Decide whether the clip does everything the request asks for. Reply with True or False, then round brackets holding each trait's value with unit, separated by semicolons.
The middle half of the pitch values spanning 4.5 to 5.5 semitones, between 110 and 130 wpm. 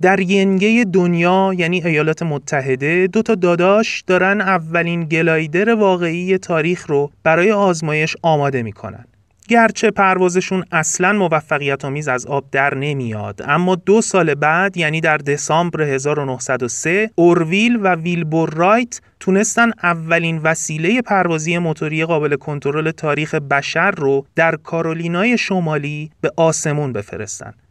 False (4.1 semitones; 120 wpm)